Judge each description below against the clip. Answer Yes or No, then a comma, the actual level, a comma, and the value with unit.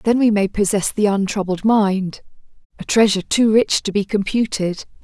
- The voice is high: Yes, high, 205 Hz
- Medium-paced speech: Yes, average, 165 wpm